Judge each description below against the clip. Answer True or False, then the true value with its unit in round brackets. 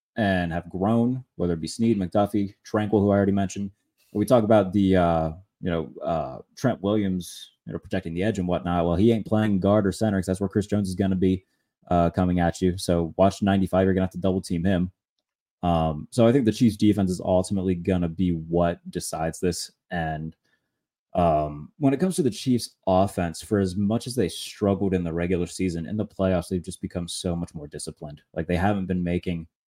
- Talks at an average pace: False (220 wpm)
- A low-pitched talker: True (95 Hz)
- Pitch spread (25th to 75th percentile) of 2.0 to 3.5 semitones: True (2.8 semitones)